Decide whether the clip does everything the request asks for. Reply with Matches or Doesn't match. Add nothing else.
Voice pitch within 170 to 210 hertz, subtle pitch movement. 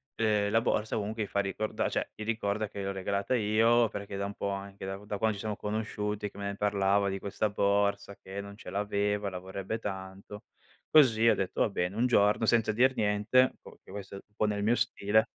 Doesn't match